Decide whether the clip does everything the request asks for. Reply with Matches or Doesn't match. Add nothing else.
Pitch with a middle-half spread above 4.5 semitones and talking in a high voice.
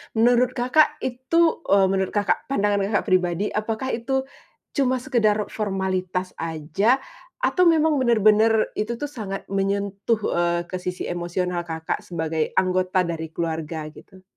Matches